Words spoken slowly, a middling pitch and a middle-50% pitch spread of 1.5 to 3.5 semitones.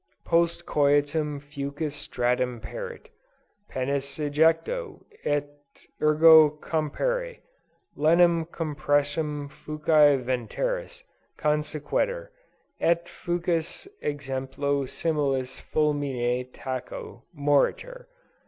Yes: slow, 70 wpm; medium, 150 Hz; average, 2.7 semitones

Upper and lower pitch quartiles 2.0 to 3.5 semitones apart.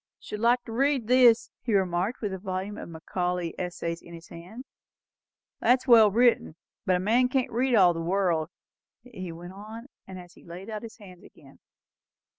No: average, 4.9 semitones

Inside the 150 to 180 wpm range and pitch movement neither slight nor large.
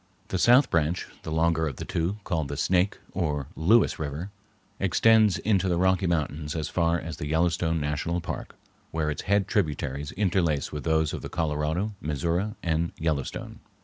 Yes: average, 170 wpm; average, 3.4 semitones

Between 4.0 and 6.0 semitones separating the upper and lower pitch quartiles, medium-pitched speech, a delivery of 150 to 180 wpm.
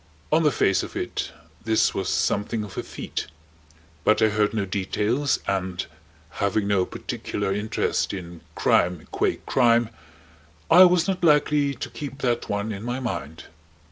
No: wide, 5.5 semitones; low, 110 Hz; average, 155 wpm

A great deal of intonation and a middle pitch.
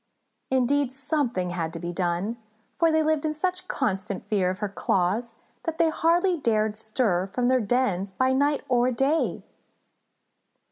No: wide, 7.0 semitones; high, 245 Hz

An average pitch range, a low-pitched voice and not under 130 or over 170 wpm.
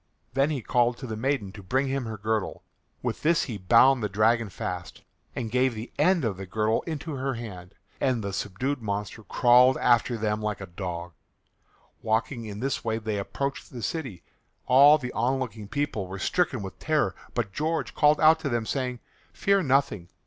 No: average, 4.4 semitones; low, 120 Hz; average, 185 wpm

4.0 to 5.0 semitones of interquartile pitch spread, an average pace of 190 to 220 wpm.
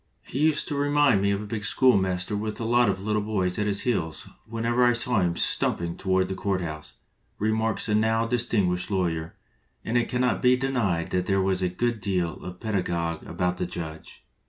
Yes: average, 4.3 semitones; fast, 205 wpm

